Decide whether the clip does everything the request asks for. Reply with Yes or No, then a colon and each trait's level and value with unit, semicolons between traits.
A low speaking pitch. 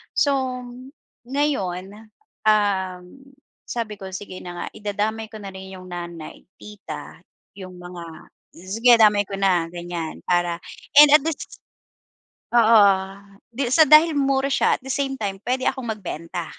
No: high, 205 Hz